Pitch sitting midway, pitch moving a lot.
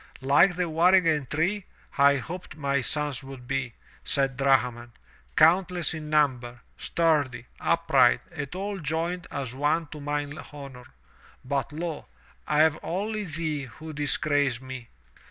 No: medium, 150 Hz; average, 3.5 semitones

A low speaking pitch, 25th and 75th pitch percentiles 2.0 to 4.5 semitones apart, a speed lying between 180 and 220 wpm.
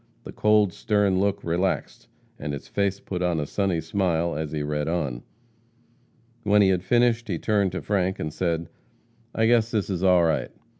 Yes: very low, 95 Hz; average, 3.7 semitones; average, 185 wpm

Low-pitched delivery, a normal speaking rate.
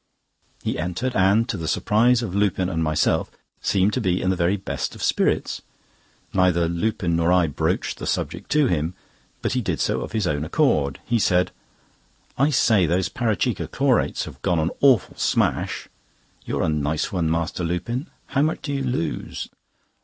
Yes: very low, 95 Hz; average, 175 wpm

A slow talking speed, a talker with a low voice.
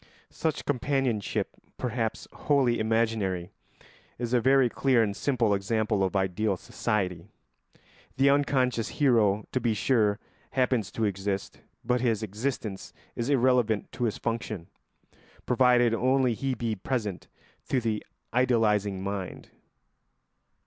Yes: slow, 120 wpm; low, 115 Hz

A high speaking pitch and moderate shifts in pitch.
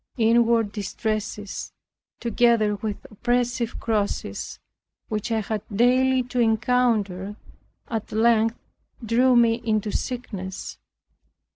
No: high, 225 Hz; narrow, 2.2 semitones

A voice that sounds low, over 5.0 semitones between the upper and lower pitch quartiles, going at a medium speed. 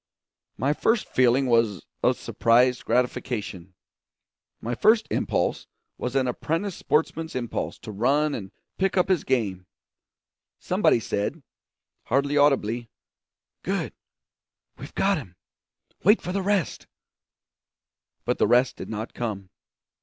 No: low, 125 Hz; wide, 5.6 semitones; slow, 120 wpm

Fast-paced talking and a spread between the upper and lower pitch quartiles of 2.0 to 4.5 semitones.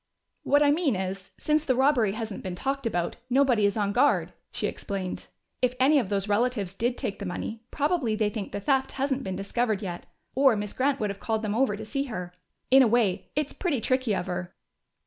No: fast, 215 wpm; average, 5.1 semitones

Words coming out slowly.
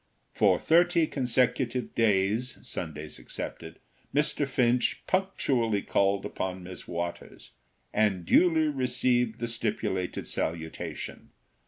Yes: slow, 100 wpm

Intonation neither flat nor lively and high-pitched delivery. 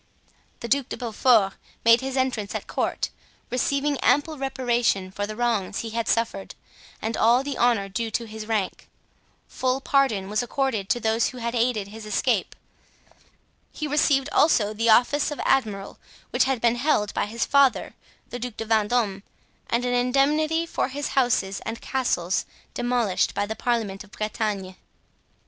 Yes: average, 3.7 semitones; high, 235 Hz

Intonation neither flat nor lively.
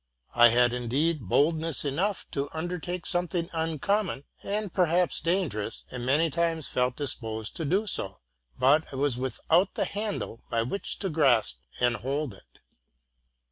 No: wide, 5.9 semitones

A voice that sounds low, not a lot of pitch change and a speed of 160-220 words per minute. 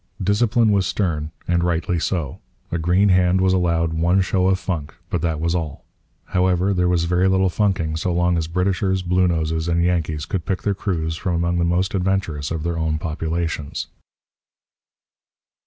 Yes: very low, 90 Hz; narrow, 2.3 semitones; average, 170 wpm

